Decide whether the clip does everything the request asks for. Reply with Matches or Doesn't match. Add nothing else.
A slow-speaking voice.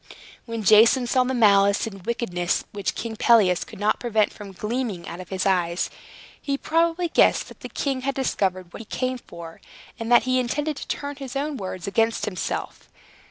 Doesn't match